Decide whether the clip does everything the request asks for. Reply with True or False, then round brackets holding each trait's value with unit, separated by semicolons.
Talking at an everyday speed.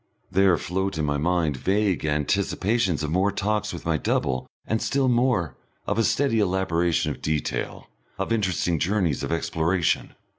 True (155 wpm)